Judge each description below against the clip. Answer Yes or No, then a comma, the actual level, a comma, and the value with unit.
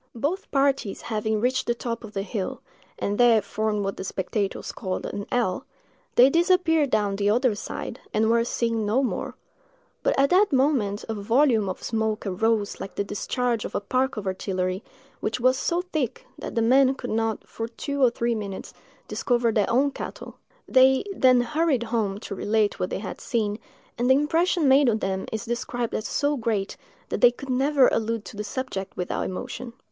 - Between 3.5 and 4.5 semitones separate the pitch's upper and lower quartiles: Yes, average, 4.0 semitones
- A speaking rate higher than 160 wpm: Yes, average, 190 wpm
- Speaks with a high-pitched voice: Yes, high, 230 Hz